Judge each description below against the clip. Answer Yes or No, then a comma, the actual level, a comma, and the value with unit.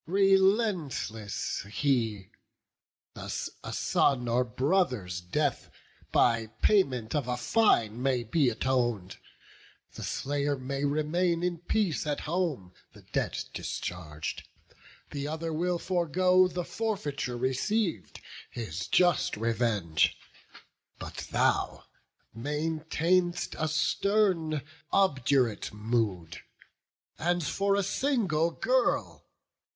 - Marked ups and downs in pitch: Yes, wide, 7.1 semitones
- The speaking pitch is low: No, medium, 145 Hz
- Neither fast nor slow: No, slow, 95 wpm